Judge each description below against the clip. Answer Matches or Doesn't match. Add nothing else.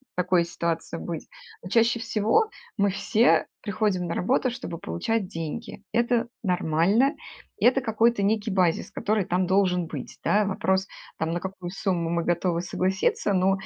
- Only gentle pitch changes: Doesn't match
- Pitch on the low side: Doesn't match